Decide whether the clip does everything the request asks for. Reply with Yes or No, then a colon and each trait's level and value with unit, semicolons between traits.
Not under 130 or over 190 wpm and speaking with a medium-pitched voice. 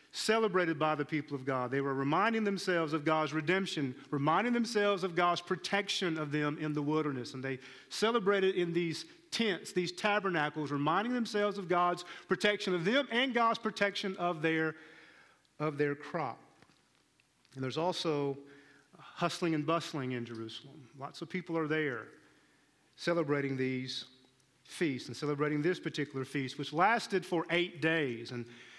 Yes: average, 150 wpm; medium, 160 Hz